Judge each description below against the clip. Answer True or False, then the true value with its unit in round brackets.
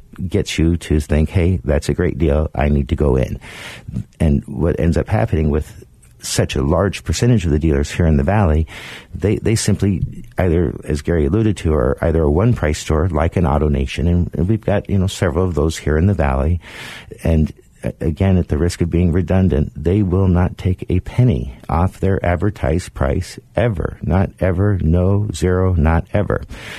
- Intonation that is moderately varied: True (4.0 semitones)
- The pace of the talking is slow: False (195 wpm)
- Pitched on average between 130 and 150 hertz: False (85 Hz)